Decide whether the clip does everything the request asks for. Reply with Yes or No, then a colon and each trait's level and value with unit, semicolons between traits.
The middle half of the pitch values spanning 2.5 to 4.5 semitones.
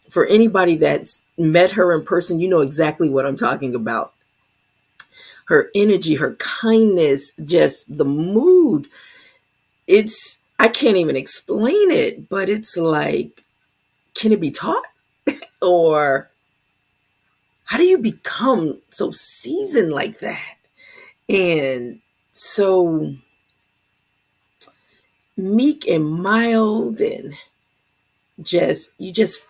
No: wide, 5.6 semitones